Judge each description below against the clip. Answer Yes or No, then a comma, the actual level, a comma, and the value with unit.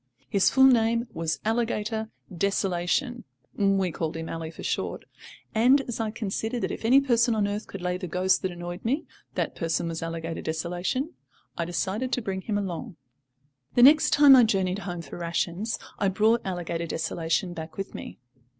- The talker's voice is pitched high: Yes, high, 195 Hz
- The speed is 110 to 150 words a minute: No, average, 175 wpm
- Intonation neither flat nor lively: Yes, average, 4.9 semitones